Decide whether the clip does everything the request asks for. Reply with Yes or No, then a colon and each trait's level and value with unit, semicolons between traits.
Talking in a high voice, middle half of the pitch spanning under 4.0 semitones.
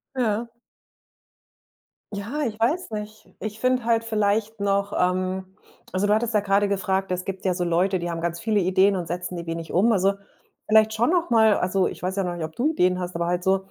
Yes: high, 195 Hz; average, 3.1 semitones